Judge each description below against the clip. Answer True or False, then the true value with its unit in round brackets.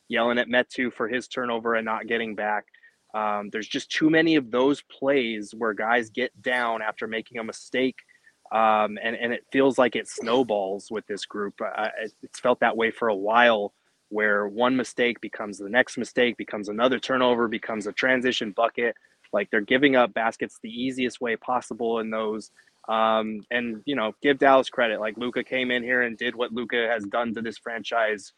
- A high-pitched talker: False (120 Hz)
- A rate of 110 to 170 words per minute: False (195 wpm)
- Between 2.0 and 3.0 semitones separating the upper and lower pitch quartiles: True (2.4 semitones)